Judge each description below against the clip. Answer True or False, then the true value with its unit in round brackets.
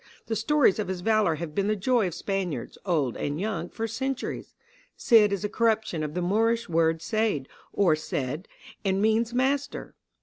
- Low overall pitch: False (205 Hz)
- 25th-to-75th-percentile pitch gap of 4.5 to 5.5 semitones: True (4.9 semitones)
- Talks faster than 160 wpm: True (175 wpm)